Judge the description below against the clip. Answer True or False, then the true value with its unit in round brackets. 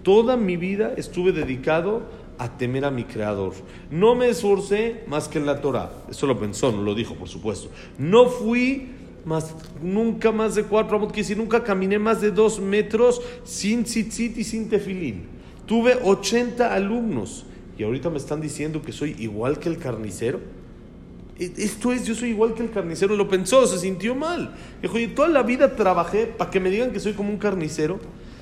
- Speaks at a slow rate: False (190 wpm)